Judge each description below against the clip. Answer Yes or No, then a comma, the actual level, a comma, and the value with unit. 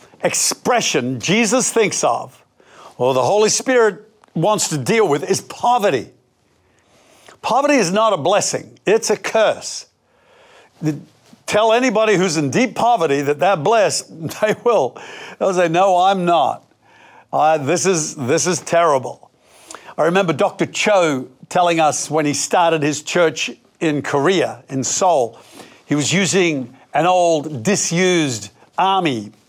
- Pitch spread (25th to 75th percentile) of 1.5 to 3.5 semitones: No, wide, 5.6 semitones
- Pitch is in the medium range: Yes, medium, 180 Hz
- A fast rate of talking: No, slow, 135 wpm